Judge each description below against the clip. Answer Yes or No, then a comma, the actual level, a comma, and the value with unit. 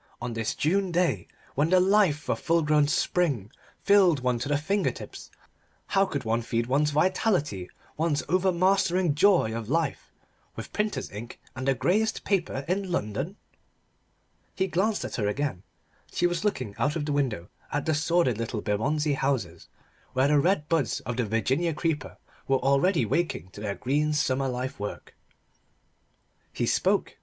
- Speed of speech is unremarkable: Yes, average, 165 wpm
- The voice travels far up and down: Yes, wide, 6.1 semitones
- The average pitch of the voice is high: No, medium, 145 Hz